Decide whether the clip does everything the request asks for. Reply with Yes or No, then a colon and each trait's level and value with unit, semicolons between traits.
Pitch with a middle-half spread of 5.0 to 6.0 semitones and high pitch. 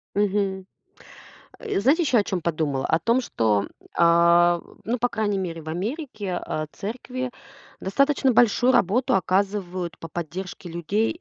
Yes: average, 5.3 semitones; high, 195 Hz